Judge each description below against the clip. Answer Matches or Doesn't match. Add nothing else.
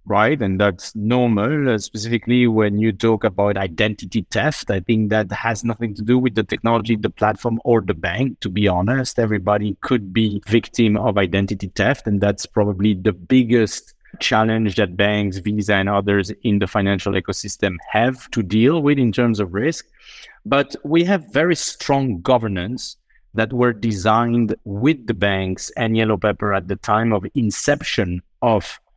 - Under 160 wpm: Doesn't match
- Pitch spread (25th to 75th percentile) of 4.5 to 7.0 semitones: Doesn't match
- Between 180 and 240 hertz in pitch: Doesn't match